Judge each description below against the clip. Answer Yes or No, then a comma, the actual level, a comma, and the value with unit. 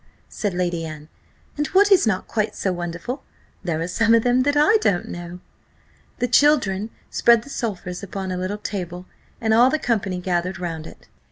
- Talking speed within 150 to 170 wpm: No, average, 185 wpm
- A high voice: Yes, high, 195 Hz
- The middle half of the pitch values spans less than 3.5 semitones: No, average, 5.3 semitones